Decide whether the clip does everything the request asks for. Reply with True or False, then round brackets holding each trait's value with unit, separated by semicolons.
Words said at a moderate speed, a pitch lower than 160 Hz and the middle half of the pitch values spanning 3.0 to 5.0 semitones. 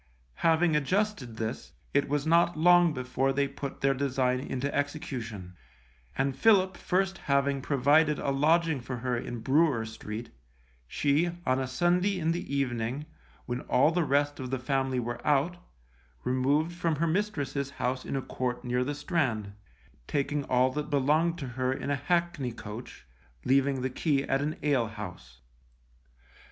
True (155 wpm; 140 Hz; 3.7 semitones)